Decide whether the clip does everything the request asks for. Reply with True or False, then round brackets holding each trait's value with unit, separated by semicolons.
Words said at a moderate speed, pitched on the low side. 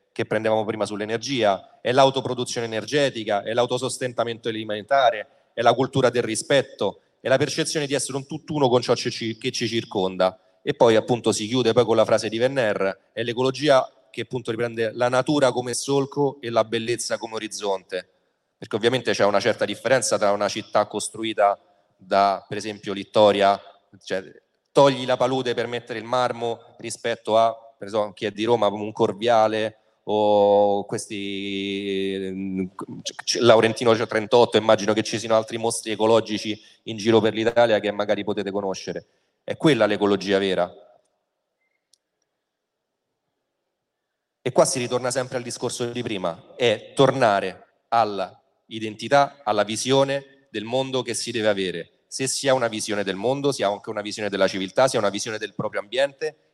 True (160 wpm; 115 Hz)